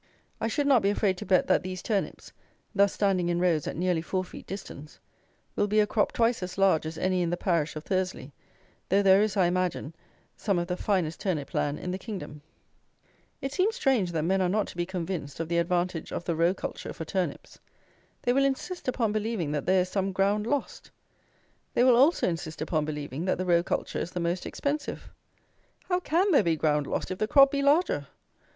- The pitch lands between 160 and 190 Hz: Yes, medium, 185 Hz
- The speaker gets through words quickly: Yes, fast, 215 wpm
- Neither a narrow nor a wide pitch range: Yes, average, 4.0 semitones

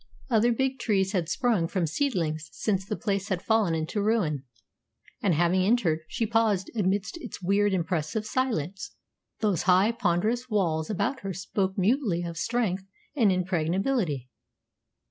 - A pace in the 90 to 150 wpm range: Yes, average, 145 wpm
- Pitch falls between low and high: No, high, 195 Hz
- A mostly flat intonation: No, average, 4.4 semitones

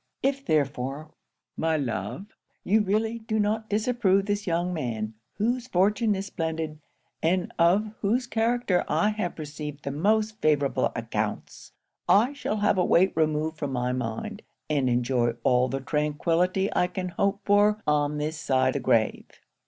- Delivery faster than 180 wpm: No, average, 150 wpm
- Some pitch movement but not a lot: No, wide, 6.5 semitones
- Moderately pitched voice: Yes, medium, 170 Hz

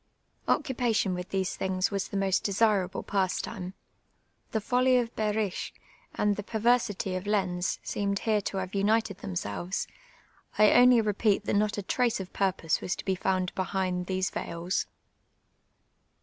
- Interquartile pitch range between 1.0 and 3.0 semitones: Yes, narrow, 2.5 semitones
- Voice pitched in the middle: No, high, 195 Hz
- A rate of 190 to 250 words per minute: No, average, 150 wpm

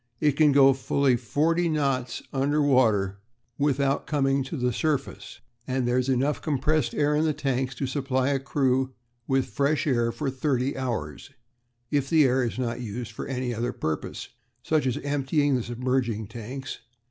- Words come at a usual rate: Yes, average, 170 wpm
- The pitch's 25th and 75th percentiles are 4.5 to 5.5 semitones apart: No, narrow, 2.6 semitones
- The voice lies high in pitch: No, low, 135 Hz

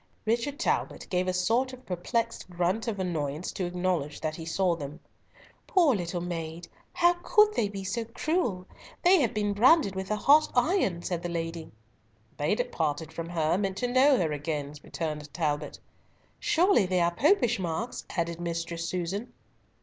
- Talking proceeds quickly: No, average, 170 wpm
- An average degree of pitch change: No, wide, 5.9 semitones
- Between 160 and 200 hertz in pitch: Yes, medium, 185 Hz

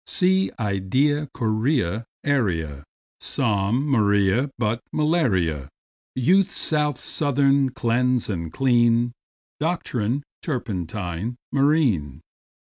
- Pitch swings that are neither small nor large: No, wide, 6.1 semitones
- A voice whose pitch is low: Yes, low, 120 Hz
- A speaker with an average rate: No, slow, 80 wpm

